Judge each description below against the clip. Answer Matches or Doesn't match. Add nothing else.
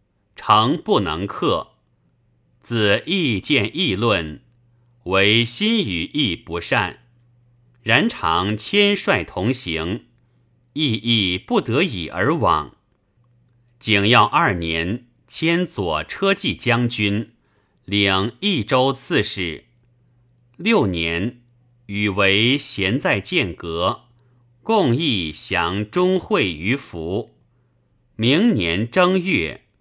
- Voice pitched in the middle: Doesn't match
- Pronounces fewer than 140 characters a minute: Matches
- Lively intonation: Doesn't match